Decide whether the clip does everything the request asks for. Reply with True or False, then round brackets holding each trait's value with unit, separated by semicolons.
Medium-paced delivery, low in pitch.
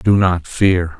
True (180 wpm; 90 Hz)